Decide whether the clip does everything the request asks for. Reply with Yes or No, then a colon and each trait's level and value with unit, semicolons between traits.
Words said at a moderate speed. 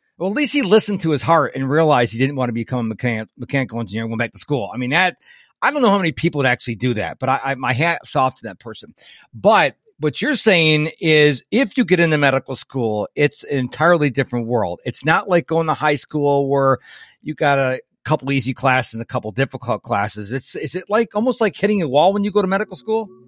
No: fast, 250 wpm